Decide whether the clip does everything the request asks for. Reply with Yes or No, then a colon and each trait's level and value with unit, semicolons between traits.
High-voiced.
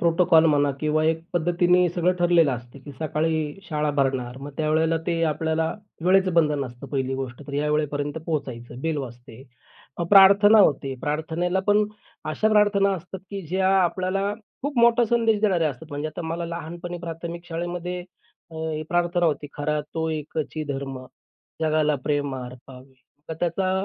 No: medium, 160 Hz